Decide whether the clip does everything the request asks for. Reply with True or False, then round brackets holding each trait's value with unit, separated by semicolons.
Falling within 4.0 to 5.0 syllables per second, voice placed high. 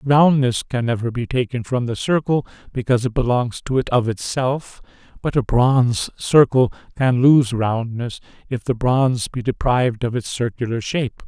False (4.9 syllables/s; 125 Hz)